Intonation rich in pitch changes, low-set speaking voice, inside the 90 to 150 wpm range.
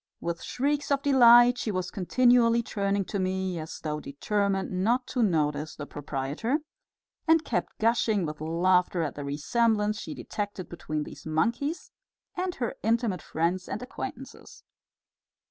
No: wide, 6.4 semitones; high, 200 Hz; average, 145 wpm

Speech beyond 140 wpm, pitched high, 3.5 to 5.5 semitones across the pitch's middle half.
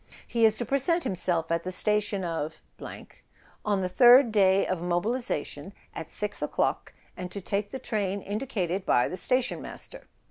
Yes: average, 165 wpm; high, 200 Hz; average, 4.4 semitones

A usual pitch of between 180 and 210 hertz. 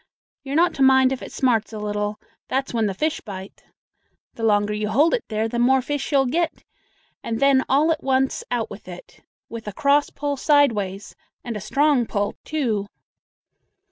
No: high, 245 Hz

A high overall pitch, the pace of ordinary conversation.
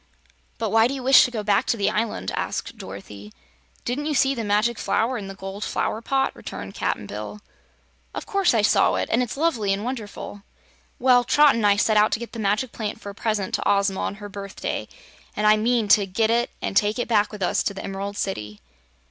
No: high, 215 Hz; fast, 225 wpm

